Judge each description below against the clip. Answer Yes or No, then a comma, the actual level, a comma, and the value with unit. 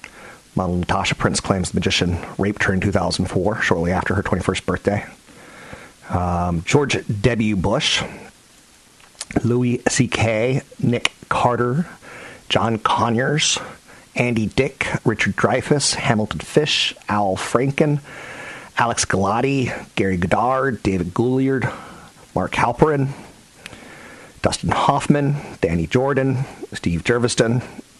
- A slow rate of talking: Yes, slow, 100 wpm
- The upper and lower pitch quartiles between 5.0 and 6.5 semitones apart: Yes, wide, 5.5 semitones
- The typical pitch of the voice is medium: No, low, 115 Hz